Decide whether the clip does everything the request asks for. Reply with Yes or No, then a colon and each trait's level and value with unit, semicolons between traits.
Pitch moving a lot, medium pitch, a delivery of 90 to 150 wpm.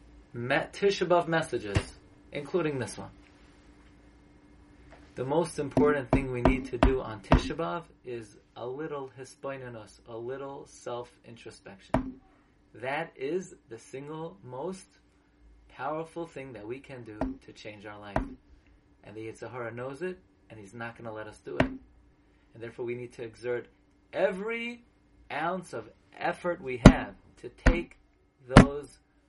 No: wide, 6.3 semitones; low, 120 Hz; slow, 135 wpm